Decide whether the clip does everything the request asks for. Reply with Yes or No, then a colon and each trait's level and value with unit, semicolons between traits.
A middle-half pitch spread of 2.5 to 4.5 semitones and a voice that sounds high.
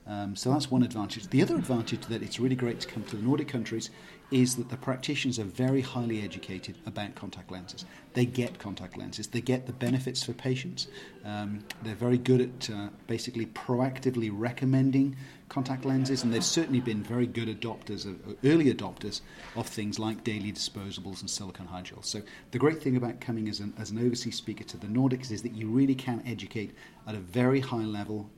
No: average, 3.4 semitones; low, 115 Hz